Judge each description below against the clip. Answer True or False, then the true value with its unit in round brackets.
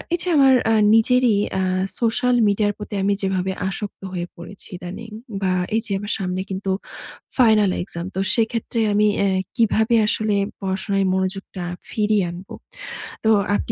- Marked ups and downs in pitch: False (2.8 semitones)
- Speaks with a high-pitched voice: True (205 Hz)